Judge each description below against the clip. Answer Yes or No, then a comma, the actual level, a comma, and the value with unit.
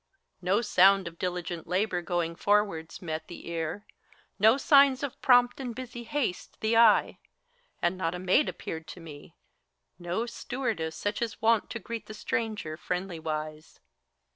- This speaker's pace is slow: No, average, 160 wpm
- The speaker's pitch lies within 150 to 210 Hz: Yes, high, 190 Hz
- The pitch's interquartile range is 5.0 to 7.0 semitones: Yes, wide, 5.5 semitones